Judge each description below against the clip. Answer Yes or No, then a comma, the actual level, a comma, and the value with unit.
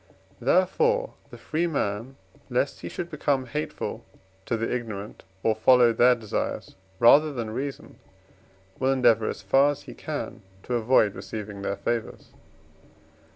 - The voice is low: Yes, low, 120 Hz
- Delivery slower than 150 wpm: Yes, average, 140 wpm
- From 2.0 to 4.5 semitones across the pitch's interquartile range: Yes, average, 4.2 semitones